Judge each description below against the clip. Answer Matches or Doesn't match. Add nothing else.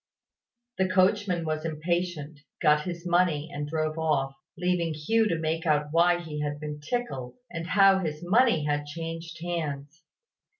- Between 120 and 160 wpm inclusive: Matches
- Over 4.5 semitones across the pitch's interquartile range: Doesn't match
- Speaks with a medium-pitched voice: Matches